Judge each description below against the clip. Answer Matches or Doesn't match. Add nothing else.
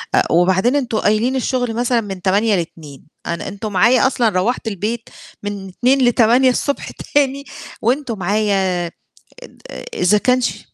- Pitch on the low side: Doesn't match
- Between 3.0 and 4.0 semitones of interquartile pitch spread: Doesn't match